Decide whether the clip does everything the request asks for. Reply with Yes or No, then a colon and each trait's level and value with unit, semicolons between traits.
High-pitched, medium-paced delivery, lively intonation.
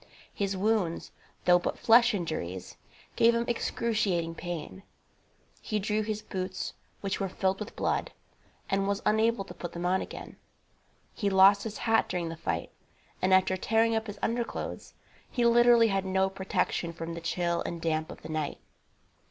No: high, 195 Hz; average, 165 wpm; average, 4.2 semitones